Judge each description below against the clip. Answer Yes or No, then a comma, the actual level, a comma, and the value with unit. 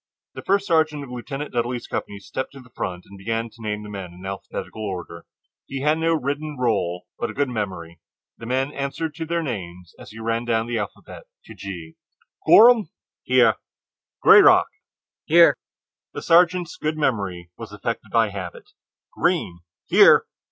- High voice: No, low, 120 Hz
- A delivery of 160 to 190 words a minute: Yes, average, 165 wpm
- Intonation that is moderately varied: No, wide, 7.4 semitones